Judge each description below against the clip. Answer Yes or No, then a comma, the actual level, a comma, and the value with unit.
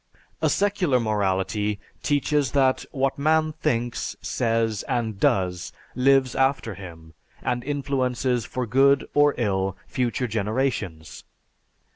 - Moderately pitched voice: No, low, 125 Hz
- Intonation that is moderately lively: Yes, average, 4.8 semitones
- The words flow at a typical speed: No, slow, 110 wpm